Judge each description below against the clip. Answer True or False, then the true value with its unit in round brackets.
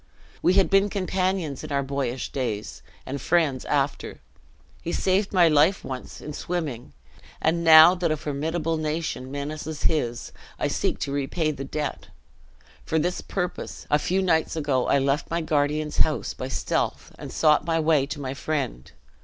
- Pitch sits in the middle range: True (155 Hz)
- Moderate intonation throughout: True (3.3 semitones)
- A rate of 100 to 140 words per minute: False (165 wpm)